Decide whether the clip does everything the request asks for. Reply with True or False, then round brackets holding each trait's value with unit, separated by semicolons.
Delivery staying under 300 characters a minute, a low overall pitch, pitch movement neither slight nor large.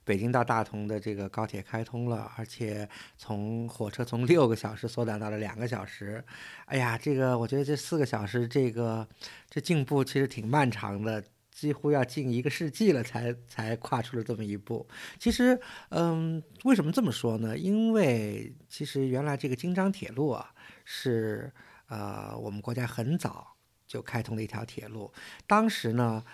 True (260 characters per minute; 120 Hz; 4.6 semitones)